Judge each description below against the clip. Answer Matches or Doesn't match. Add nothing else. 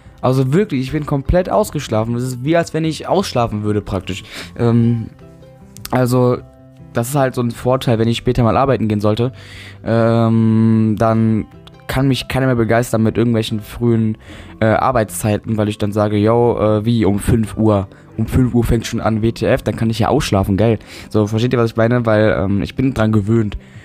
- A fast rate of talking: Matches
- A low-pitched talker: Matches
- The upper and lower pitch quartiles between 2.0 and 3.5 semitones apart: Matches